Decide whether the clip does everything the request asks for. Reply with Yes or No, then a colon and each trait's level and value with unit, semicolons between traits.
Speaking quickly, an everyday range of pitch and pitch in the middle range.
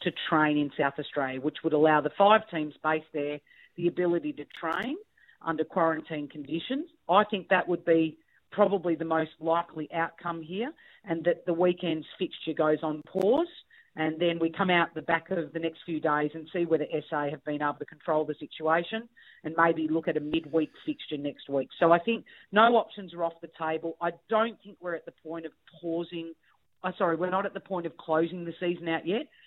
No: fast, 210 wpm; narrow, 2.3 semitones; medium, 165 Hz